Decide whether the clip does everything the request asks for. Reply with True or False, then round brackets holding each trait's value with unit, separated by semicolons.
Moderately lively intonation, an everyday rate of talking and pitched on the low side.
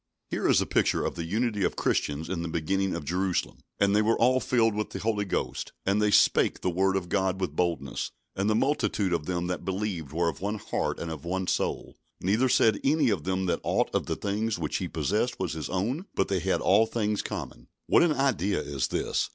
False (3.7 semitones; 230 wpm; 95 Hz)